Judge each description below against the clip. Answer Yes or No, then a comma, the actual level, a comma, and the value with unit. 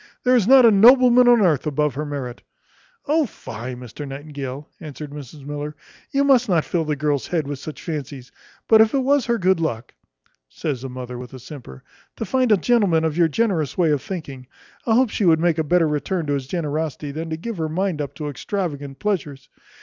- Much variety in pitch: Yes, wide, 6.0 semitones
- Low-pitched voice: No, medium, 155 Hz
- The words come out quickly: Yes, fast, 210 wpm